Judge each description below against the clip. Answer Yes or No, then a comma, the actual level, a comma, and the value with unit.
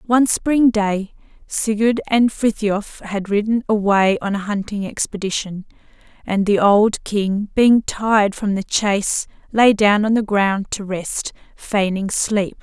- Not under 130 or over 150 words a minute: Yes, average, 145 wpm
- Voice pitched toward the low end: No, high, 210 Hz